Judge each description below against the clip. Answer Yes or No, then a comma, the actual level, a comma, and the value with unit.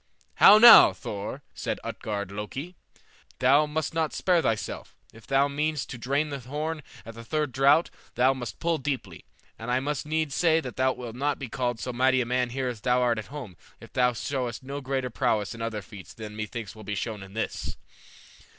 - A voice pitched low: Yes, low, 130 Hz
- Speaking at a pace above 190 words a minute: Yes, fast, 205 wpm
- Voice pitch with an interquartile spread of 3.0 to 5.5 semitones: Yes, average, 4.3 semitones